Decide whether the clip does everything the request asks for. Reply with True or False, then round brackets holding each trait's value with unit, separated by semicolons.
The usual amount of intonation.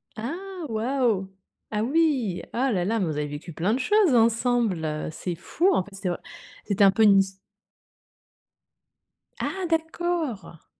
False (6.8 semitones)